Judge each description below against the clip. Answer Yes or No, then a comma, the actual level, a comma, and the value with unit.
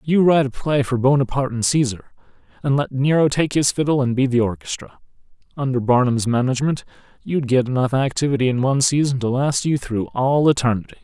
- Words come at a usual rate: Yes, average, 185 wpm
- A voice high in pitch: No, low, 130 Hz